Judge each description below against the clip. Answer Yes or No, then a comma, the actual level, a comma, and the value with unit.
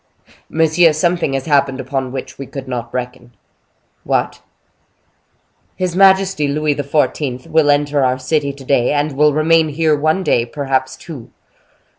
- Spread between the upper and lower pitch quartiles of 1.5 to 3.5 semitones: Yes, average, 3.1 semitones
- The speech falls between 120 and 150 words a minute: Yes, average, 145 wpm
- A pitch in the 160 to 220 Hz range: No, medium, 145 Hz